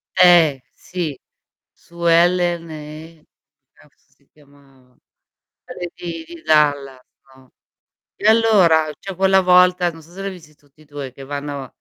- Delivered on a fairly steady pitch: No, average, 3.6 semitones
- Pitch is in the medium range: Yes, medium, 160 Hz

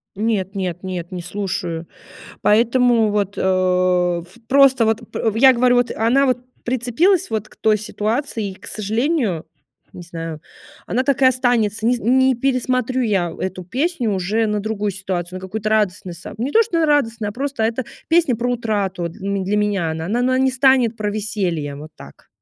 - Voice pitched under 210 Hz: No, high, 220 Hz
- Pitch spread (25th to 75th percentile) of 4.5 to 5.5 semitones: Yes, average, 4.8 semitones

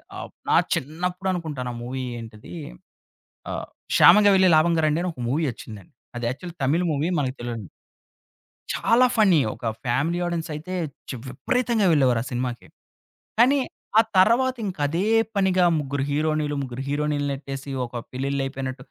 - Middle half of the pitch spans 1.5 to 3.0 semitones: No, wide, 5.6 semitones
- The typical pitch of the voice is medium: Yes, medium, 150 Hz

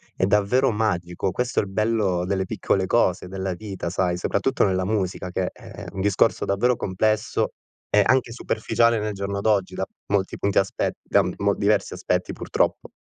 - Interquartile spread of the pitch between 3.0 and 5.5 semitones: No, narrow, 2.5 semitones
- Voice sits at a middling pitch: No, low, 100 Hz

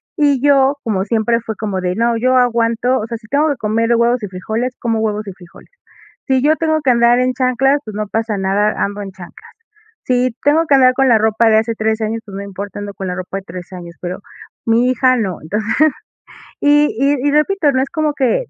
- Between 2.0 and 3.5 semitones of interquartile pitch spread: No, average, 4.0 semitones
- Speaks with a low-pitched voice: No, high, 230 Hz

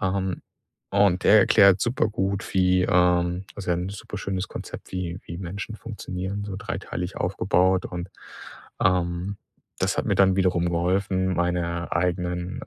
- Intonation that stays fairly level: Yes, narrow, 1.7 semitones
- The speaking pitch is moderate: No, very low, 90 Hz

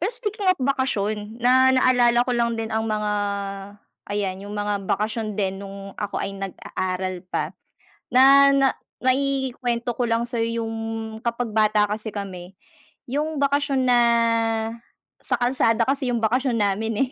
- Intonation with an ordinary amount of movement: Yes, average, 3.9 semitones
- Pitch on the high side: Yes, high, 230 Hz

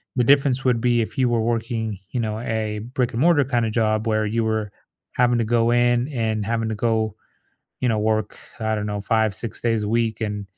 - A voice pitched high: No, low, 115 Hz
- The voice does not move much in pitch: Yes, narrow, 1.8 semitones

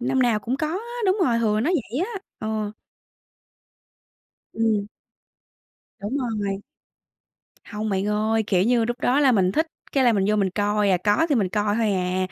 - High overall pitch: Yes, high, 215 Hz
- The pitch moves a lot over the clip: No, average, 3.3 semitones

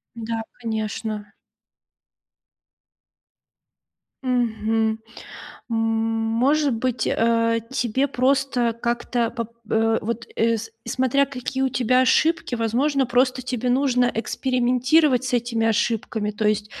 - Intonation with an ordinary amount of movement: No, narrow, 2.3 semitones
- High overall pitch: Yes, high, 235 Hz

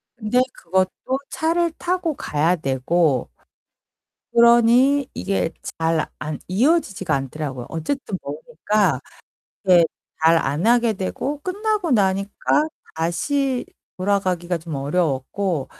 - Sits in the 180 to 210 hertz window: Yes, high, 190 Hz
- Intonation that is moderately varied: No, wide, 7.4 semitones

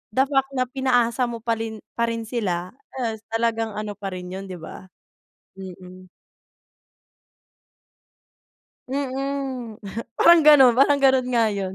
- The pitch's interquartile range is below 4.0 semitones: No, average, 4.7 semitones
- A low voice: No, high, 230 Hz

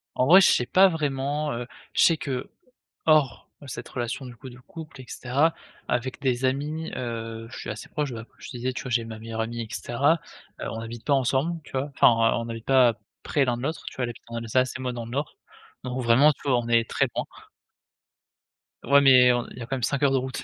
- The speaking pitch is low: Yes, low, 125 Hz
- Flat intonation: No, average, 3.0 semitones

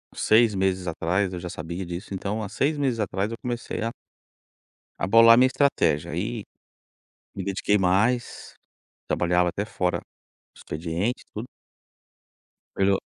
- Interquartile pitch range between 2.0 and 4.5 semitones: Yes, average, 4.2 semitones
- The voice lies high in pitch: No, low, 100 Hz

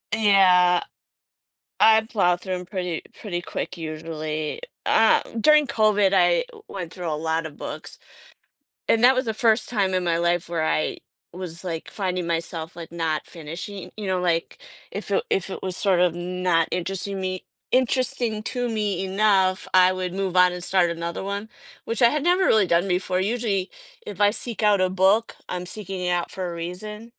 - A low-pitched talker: No, medium, 185 Hz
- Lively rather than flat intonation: No, average, 3.4 semitones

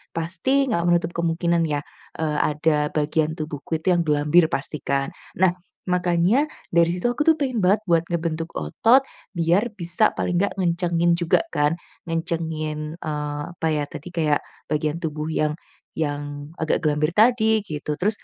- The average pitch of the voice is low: No, medium, 165 Hz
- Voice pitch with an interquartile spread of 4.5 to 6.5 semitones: No, narrow, 2.6 semitones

